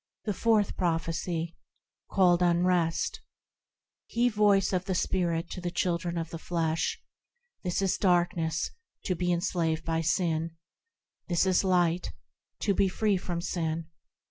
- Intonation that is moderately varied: No, narrow, 2.1 semitones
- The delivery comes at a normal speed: No, slow, 125 wpm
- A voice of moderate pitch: Yes, medium, 175 Hz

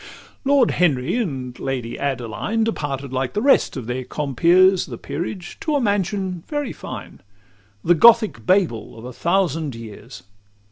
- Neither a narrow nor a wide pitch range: No, wide, 7.8 semitones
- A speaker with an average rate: Yes, average, 155 wpm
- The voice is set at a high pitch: No, medium, 165 Hz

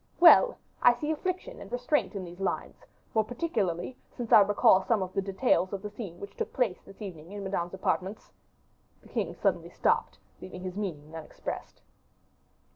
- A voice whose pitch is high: Yes, high, 200 Hz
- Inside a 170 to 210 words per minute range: Yes, average, 180 wpm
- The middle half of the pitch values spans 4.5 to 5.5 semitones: Yes, average, 4.8 semitones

